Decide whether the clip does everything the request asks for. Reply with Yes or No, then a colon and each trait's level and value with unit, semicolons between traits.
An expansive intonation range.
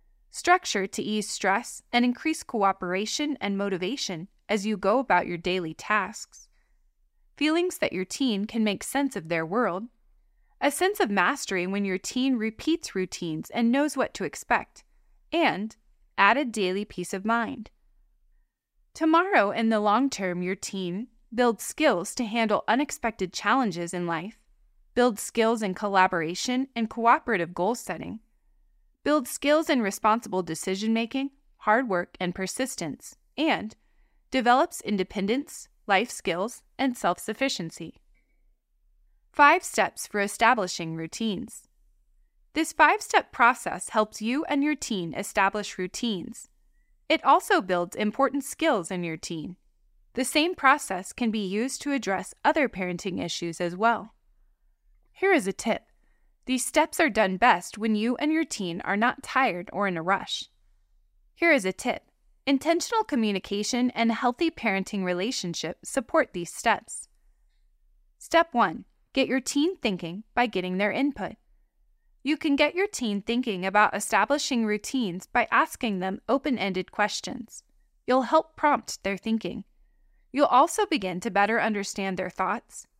Yes: wide, 6.1 semitones